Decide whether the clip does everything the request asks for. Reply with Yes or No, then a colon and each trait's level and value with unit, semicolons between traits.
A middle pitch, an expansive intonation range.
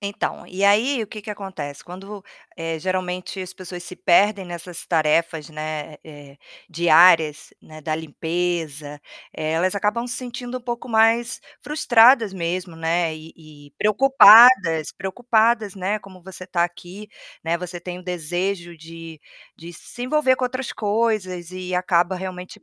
No: medium, 180 Hz; average, 4.2 semitones